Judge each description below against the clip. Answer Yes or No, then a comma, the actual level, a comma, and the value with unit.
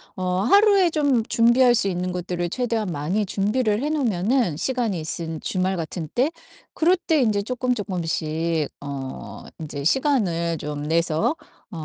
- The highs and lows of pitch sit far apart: Yes, wide, 7.1 semitones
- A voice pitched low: No, high, 195 Hz